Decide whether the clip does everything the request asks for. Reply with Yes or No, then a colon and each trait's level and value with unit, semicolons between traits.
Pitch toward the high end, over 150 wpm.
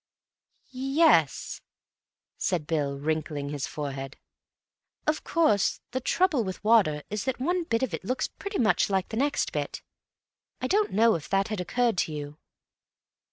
Yes: high, 195 Hz; average, 160 wpm